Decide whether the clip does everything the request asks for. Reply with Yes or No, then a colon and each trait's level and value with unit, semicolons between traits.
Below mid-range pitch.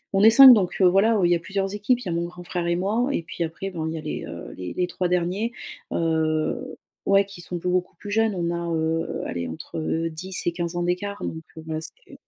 No: medium, 175 Hz